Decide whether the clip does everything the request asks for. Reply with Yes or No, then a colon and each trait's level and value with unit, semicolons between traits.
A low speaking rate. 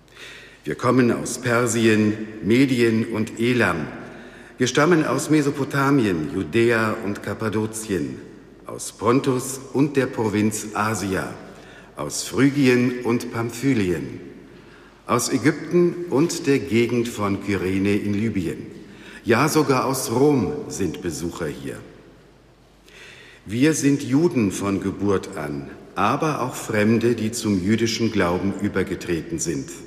Yes: slow, 110 wpm